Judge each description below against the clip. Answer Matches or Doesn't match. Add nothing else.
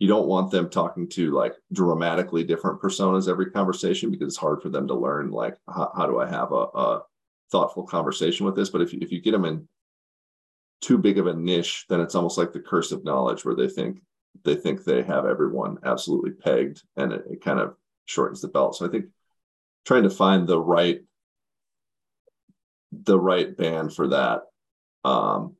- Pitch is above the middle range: Doesn't match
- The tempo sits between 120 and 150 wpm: Doesn't match